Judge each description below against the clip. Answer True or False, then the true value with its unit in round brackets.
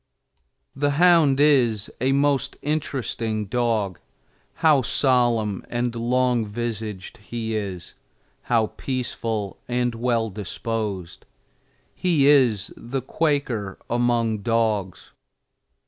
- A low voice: True (120 Hz)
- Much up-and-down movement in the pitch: False (3.5 semitones)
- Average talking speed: False (95 wpm)